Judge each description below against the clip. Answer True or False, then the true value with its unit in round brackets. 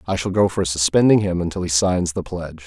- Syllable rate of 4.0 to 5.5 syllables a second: False (6.0 syllables/s)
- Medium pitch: False (90 Hz)